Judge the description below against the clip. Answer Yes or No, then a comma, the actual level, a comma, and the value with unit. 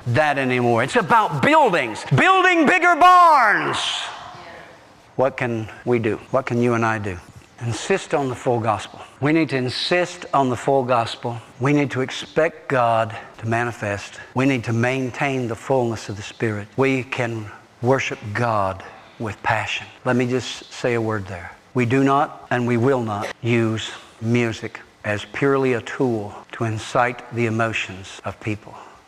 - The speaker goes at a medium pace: Yes, average, 165 wpm